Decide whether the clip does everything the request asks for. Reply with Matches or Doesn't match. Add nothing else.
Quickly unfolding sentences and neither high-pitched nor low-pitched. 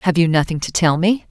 Matches